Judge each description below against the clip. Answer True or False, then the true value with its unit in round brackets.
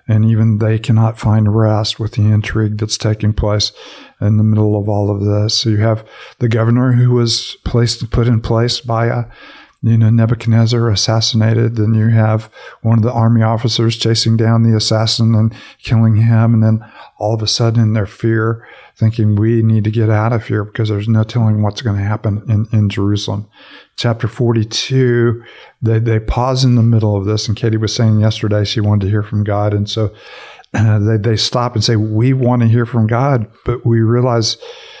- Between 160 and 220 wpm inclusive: True (200 wpm)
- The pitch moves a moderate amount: False (1.4 semitones)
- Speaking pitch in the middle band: False (110 Hz)